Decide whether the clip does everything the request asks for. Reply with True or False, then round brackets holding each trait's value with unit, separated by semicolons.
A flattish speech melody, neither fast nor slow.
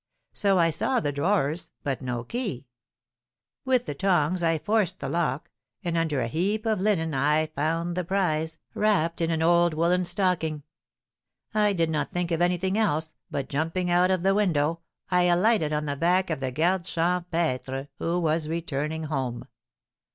False (3.0 semitones; 175 wpm)